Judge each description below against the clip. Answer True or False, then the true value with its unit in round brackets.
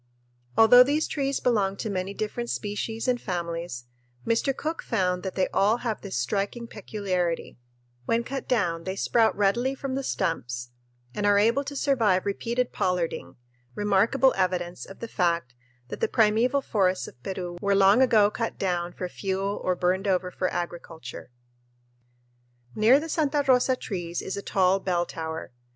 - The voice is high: True (200 Hz)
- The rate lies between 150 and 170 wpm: True (160 wpm)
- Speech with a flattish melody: False (4.6 semitones)